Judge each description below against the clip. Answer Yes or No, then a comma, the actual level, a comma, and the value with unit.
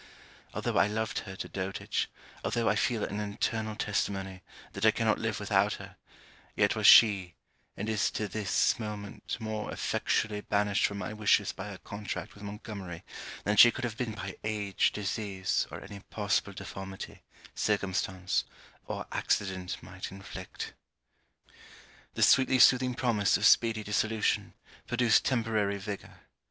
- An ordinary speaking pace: Yes, average, 145 wpm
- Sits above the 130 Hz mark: No, low, 105 Hz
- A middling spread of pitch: No, narrow, 2.0 semitones